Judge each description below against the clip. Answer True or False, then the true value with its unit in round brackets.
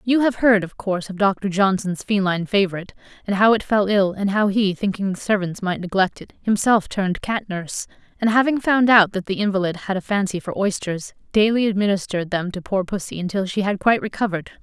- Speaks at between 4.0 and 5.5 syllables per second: False (5.9 syllables/s)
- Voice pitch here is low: False (200 Hz)